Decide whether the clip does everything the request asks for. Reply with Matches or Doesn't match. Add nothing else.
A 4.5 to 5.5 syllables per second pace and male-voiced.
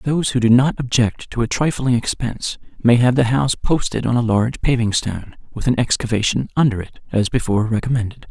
Doesn't match